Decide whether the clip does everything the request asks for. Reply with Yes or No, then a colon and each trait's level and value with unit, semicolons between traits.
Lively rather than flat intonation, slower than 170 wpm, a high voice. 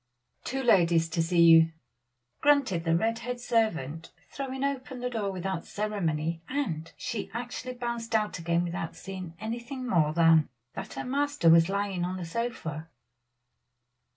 Yes: wide, 6.6 semitones; average, 150 wpm; high, 195 Hz